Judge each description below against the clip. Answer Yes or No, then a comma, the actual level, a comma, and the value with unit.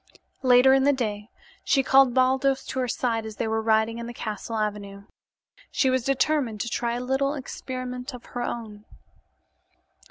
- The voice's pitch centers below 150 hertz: No, high, 245 Hz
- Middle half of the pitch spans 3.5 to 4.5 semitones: No, average, 3.1 semitones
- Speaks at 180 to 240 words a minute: No, average, 170 wpm